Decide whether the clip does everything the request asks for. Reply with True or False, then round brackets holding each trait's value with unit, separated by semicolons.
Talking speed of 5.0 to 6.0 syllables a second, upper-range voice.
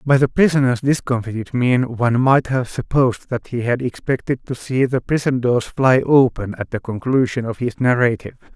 False (5.2 syllables/s; 125 Hz)